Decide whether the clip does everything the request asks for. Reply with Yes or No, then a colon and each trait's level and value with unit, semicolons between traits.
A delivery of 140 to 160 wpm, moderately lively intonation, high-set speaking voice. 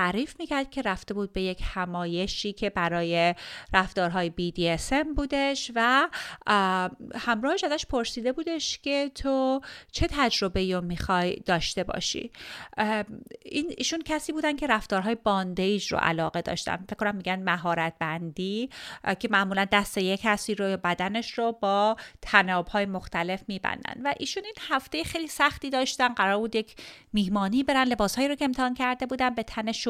No: average, 150 wpm; wide, 6.2 semitones; high, 215 Hz